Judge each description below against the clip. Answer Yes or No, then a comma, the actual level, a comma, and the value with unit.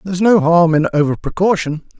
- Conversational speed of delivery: No, fast, 210 wpm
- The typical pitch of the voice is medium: Yes, medium, 175 Hz